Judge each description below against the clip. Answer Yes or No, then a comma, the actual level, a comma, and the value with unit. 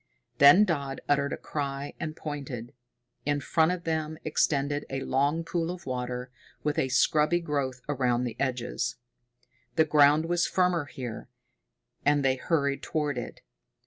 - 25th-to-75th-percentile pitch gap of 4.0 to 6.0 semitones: No, average, 3.1 semitones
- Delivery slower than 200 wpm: Yes, average, 145 wpm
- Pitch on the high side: No, medium, 145 Hz